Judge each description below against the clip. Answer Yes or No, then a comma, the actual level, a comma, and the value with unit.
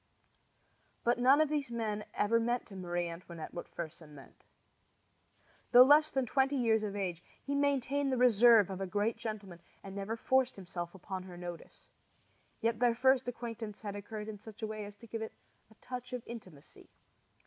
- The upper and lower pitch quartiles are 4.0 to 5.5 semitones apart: Yes, average, 4.3 semitones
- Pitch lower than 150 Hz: No, high, 220 Hz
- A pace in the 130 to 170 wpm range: No, average, 185 wpm